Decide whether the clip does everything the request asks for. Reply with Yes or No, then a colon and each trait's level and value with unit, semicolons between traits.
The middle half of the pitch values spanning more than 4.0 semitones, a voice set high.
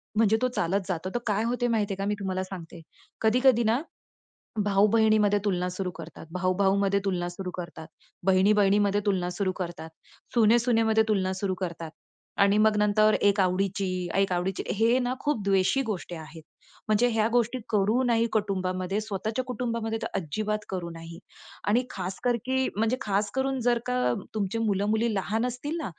No: average, 3.2 semitones; high, 205 Hz